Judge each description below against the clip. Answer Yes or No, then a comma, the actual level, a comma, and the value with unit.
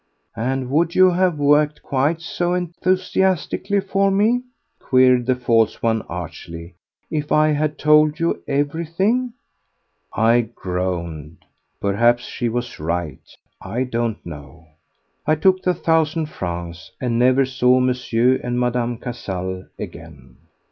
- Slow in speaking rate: Yes, slow, 125 wpm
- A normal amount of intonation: No, wide, 7.4 semitones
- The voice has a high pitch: No, low, 130 Hz